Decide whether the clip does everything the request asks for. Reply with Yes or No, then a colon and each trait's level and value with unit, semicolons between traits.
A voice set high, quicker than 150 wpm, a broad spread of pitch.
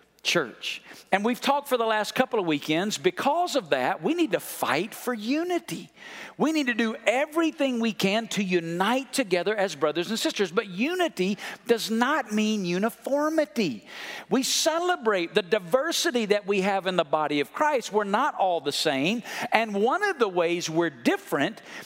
Yes: high, 225 Hz; average, 175 wpm; wide, 6.6 semitones